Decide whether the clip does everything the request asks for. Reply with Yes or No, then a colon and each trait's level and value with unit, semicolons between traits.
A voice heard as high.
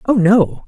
Yes: high, 195 Hz